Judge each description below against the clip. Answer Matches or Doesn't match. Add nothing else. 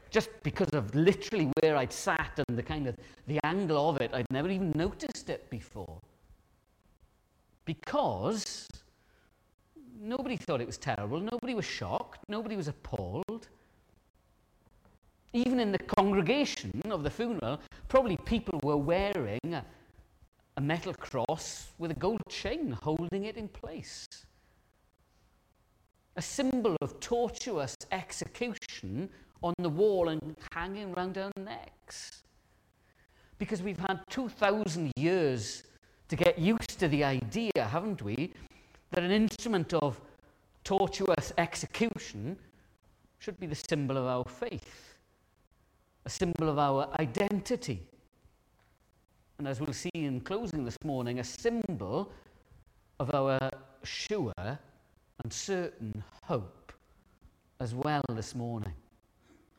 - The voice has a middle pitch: Matches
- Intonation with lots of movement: Matches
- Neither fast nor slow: Doesn't match